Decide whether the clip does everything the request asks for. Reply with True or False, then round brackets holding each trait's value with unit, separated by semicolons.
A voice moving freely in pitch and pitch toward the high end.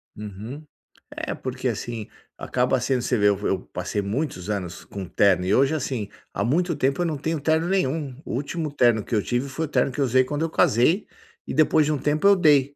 False (6.0 semitones; 130 Hz)